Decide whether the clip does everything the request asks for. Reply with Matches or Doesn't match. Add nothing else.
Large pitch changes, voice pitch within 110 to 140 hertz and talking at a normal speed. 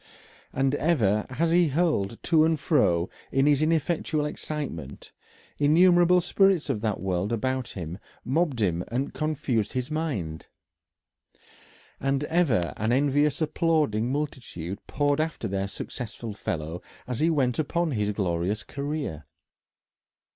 Doesn't match